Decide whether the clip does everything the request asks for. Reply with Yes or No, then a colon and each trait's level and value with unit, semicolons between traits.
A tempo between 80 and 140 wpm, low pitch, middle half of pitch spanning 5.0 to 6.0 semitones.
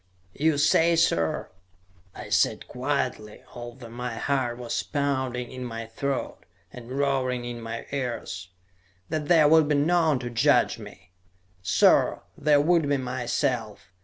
No: slow, 135 wpm; low, 130 Hz; average, 3.3 semitones